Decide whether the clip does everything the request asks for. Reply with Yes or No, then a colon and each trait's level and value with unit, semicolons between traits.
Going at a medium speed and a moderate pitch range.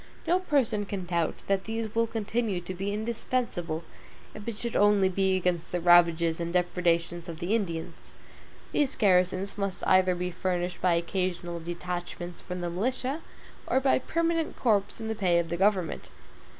Yes: average, 165 wpm; average, 3.8 semitones